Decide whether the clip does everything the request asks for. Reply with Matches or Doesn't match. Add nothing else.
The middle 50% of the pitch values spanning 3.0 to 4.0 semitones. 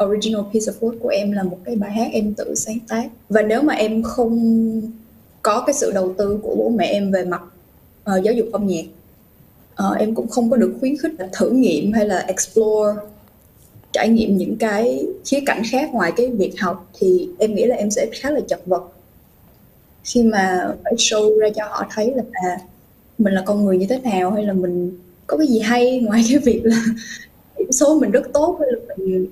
Matches